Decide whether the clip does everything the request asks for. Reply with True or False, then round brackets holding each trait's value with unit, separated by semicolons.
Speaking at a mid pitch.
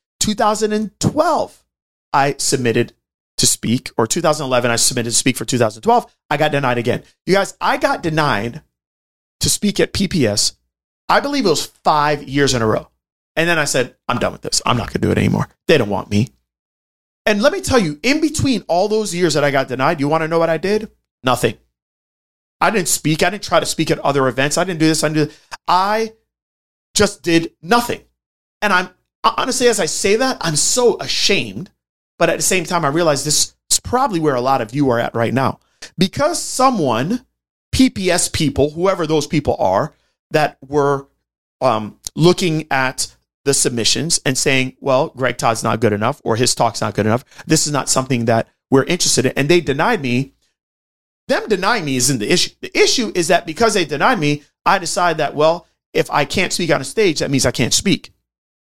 True (150 Hz)